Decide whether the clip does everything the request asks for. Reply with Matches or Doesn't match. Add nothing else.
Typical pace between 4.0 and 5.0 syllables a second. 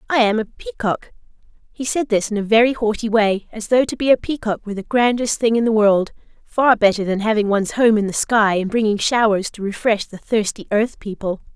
Doesn't match